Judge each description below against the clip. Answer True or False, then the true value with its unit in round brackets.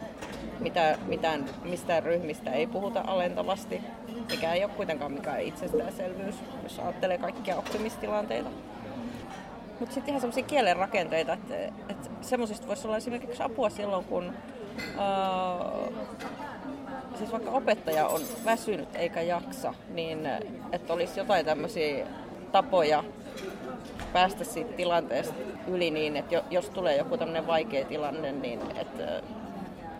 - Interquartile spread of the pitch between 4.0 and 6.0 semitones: True (5.3 semitones)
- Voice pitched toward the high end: True (210 Hz)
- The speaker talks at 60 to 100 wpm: False (120 wpm)